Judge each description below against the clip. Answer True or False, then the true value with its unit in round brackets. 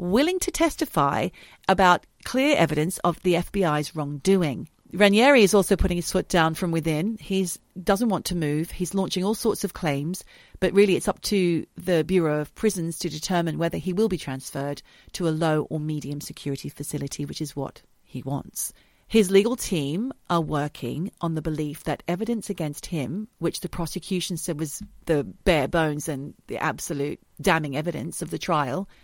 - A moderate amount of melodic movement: True (4.1 semitones)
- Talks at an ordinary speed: True (180 wpm)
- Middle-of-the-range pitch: True (175 Hz)